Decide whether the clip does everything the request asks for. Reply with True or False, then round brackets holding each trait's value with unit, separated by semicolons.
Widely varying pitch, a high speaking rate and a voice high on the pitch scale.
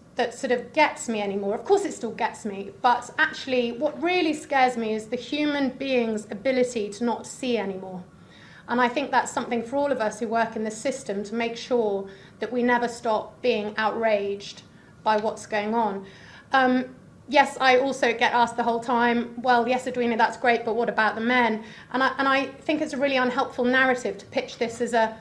False (3.0 semitones; 210 wpm; 240 Hz)